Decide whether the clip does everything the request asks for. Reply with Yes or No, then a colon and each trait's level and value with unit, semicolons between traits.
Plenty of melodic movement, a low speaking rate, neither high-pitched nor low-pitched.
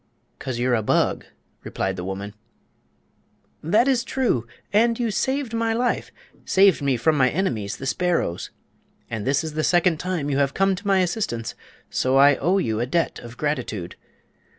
No: wide, 8.3 semitones; average, 170 wpm; medium, 150 Hz